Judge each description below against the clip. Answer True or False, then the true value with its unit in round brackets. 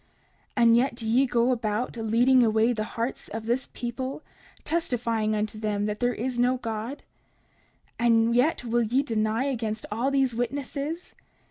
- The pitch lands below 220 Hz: False (235 Hz)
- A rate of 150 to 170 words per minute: True (155 wpm)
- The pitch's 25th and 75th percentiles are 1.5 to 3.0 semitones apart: True (2.6 semitones)